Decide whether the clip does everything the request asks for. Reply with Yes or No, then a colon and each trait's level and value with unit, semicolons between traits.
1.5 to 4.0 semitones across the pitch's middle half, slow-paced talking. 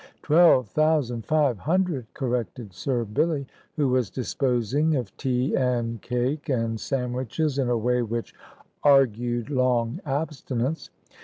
Yes: average, 3.3 semitones; slow, 125 wpm